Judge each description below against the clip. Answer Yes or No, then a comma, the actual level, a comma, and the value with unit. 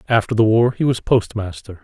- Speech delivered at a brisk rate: No, average, 195 wpm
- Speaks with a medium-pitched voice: No, low, 110 Hz